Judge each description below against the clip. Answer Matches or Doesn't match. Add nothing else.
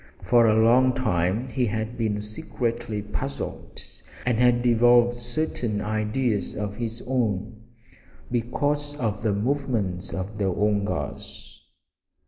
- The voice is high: Doesn't match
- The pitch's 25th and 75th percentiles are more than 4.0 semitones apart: Doesn't match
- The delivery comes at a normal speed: Doesn't match